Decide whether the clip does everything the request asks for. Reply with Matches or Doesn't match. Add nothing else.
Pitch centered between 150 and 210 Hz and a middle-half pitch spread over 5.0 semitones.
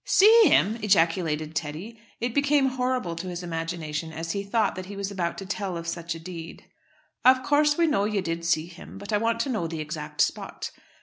Matches